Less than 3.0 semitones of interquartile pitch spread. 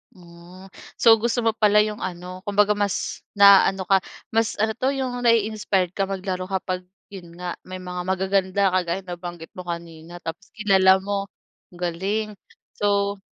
Yes: narrow, 2.4 semitones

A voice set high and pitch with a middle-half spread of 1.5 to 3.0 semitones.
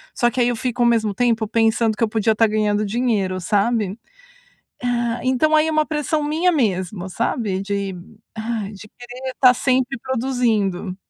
No: high, 230 Hz; average, 3.4 semitones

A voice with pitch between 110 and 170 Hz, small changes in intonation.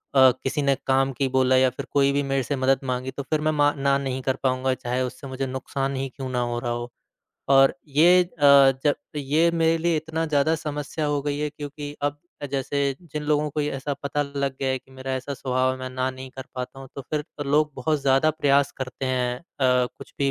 Yes: low, 135 Hz; narrow, 2.0 semitones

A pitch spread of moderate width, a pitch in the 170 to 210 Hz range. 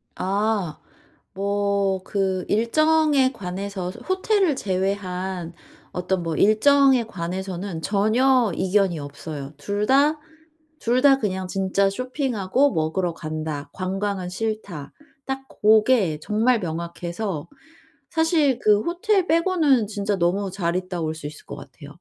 No: wide, 5.9 semitones; high, 200 Hz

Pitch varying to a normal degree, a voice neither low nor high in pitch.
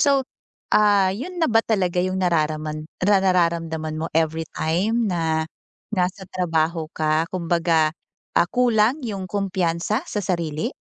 Yes: average, 4.2 semitones; medium, 180 Hz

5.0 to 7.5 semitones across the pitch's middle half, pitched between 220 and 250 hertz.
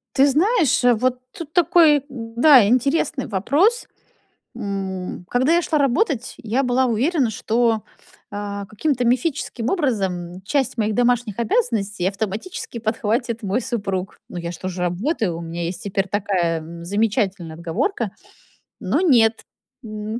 Yes: wide, 5.4 semitones; high, 225 Hz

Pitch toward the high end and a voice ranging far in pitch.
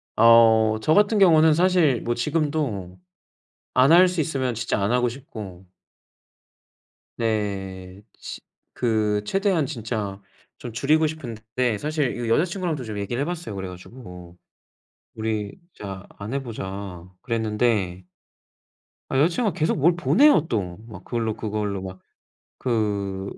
No: low, 115 Hz; wide, 6.9 semitones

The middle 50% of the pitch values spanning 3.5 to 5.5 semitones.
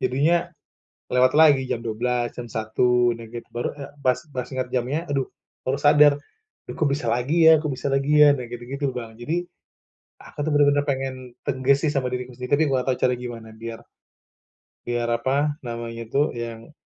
No: average, 3.0 semitones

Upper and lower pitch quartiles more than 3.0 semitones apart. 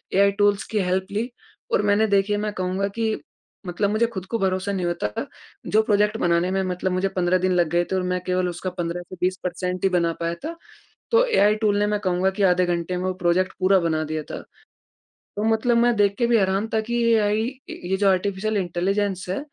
No: narrow, 2.4 semitones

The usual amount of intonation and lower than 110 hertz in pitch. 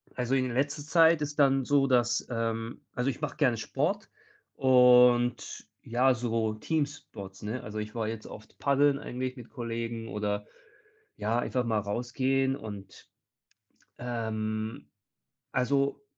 No: average, 3.3 semitones; low, 125 Hz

